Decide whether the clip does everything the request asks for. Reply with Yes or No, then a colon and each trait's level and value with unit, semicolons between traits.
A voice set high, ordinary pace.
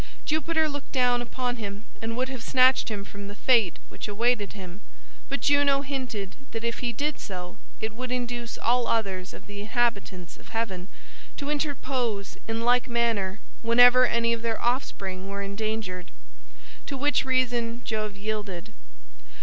Yes: high, 230 Hz; average, 160 wpm